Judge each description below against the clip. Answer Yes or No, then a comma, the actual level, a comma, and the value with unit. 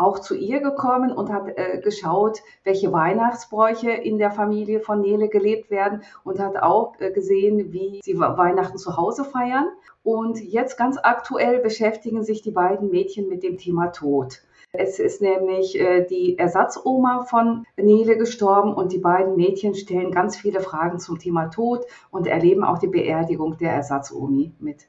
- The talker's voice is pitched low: No, high, 195 Hz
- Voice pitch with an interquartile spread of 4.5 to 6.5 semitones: No, average, 3.6 semitones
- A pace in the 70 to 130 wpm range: No, average, 165 wpm